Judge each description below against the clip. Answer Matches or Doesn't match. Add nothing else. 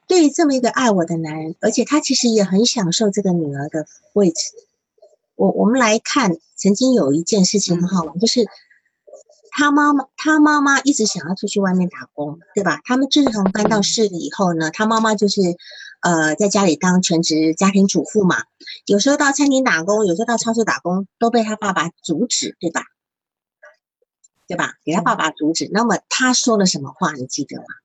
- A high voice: Matches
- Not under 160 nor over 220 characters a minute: Doesn't match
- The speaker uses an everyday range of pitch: Doesn't match